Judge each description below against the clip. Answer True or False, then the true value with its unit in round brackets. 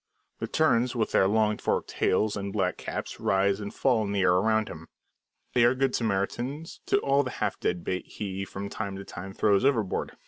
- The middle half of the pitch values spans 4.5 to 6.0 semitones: False (3.7 semitones)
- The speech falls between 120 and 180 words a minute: False (205 wpm)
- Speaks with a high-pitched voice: False (105 Hz)